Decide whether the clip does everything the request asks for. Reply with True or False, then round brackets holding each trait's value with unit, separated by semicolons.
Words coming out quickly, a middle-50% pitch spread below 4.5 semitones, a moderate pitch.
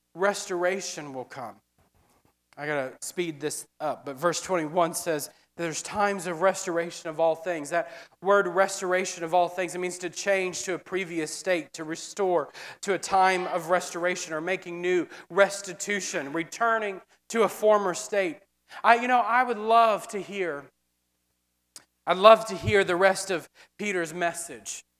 False (160 wpm; 2.8 semitones; 180 Hz)